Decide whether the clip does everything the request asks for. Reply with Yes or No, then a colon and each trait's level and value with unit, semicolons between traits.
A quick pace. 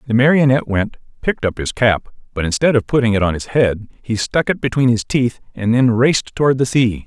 Yes: fast, 220 wpm